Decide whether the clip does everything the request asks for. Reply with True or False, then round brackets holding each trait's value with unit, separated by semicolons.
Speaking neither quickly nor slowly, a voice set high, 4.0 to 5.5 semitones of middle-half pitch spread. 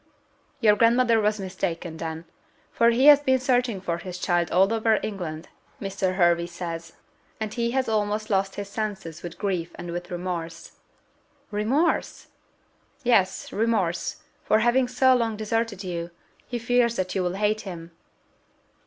True (150 wpm; 205 Hz; 4.7 semitones)